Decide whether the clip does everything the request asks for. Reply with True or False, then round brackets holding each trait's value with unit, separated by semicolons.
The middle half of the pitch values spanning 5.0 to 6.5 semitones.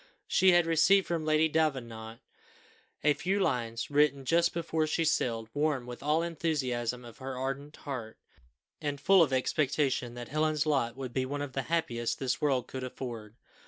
False (4.0 semitones)